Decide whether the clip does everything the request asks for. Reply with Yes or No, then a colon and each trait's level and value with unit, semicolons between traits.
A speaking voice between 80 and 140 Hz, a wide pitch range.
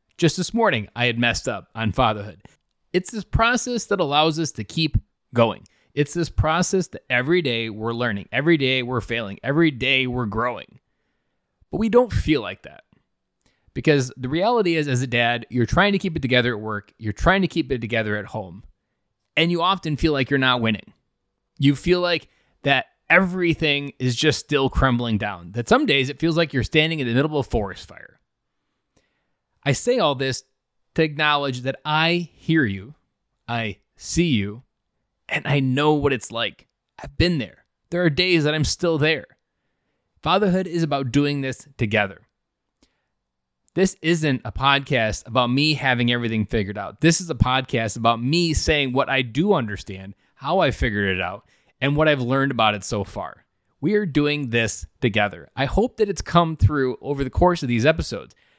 Yes: low, 135 Hz; wide, 5.7 semitones